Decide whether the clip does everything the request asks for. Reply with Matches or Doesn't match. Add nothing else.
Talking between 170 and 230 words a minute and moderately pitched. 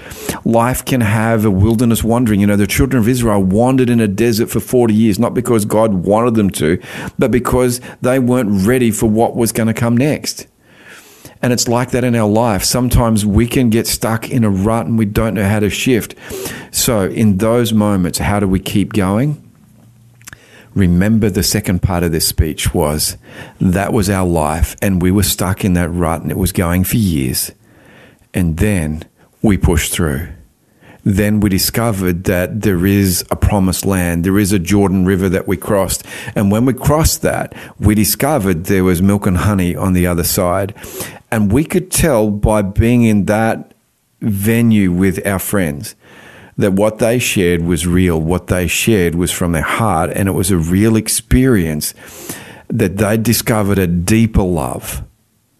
Doesn't match